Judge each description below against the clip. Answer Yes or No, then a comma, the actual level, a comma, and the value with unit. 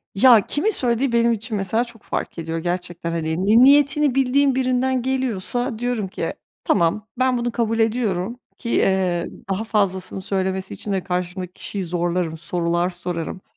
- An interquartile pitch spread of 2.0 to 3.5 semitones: No, wide, 5.5 semitones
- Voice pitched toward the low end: No, high, 205 Hz